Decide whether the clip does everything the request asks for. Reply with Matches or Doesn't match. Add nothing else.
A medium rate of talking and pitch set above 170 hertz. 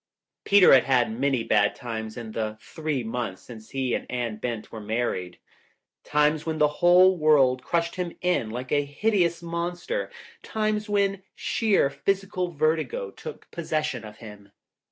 Doesn't match